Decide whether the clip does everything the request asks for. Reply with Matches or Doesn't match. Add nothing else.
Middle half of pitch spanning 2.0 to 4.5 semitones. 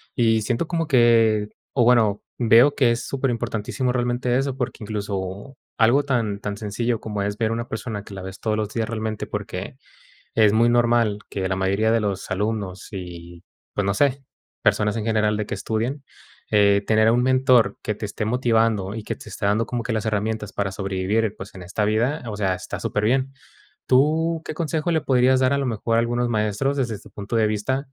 Matches